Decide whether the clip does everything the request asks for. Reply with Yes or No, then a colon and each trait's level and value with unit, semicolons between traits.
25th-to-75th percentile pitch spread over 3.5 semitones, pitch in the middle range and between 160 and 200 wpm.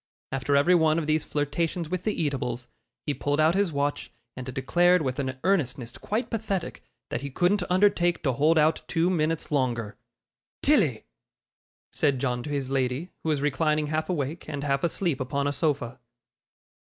Yes: average, 4.1 semitones; medium, 150 Hz; average, 170 wpm